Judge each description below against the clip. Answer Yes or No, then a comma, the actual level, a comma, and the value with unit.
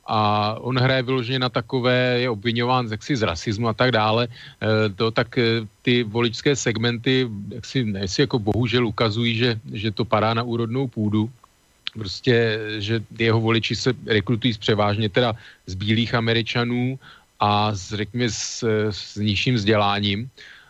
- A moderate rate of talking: Yes, average, 150 wpm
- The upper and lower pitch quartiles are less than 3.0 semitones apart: Yes, narrow, 2.5 semitones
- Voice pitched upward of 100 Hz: Yes, low, 115 Hz